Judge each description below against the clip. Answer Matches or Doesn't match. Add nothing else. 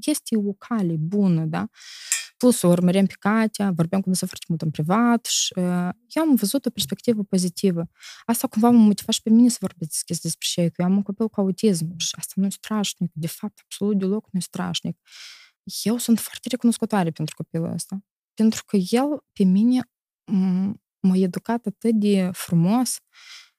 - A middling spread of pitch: Matches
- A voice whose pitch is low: Doesn't match